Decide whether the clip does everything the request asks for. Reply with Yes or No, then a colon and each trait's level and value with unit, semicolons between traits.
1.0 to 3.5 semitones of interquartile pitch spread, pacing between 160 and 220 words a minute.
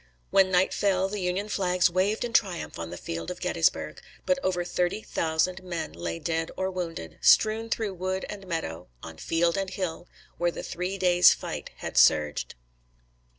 Yes: average, 2.7 semitones; average, 175 wpm